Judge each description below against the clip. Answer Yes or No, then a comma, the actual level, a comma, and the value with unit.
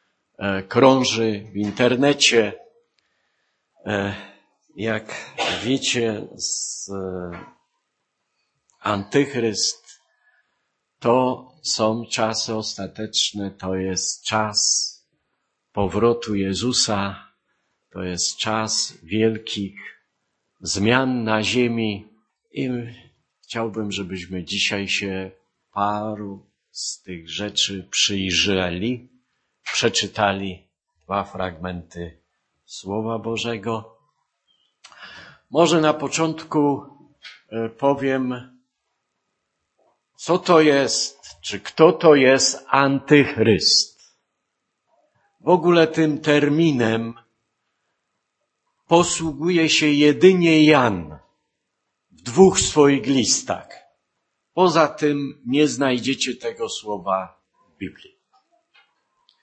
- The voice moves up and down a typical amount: No, wide, 6.2 semitones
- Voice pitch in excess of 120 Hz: No, low, 115 Hz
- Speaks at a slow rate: Yes, slow, 70 wpm